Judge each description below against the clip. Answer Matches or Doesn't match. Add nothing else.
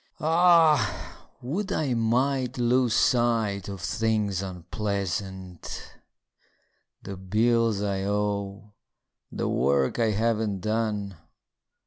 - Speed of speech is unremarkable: Doesn't match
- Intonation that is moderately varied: Matches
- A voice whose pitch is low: Matches